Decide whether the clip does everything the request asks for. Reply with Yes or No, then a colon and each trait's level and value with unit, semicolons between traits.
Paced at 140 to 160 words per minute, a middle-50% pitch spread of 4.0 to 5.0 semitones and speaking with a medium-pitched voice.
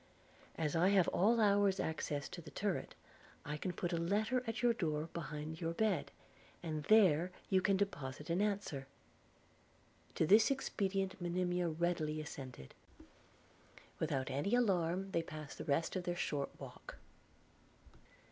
Yes: average, 145 wpm; average, 4.4 semitones; medium, 175 Hz